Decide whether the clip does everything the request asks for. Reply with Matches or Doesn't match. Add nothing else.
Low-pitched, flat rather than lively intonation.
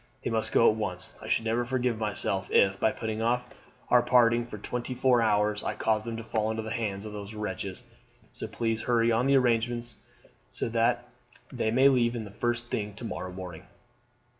Matches